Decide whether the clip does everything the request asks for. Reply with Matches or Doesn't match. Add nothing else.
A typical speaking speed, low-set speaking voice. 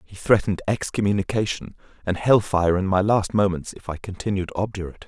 Matches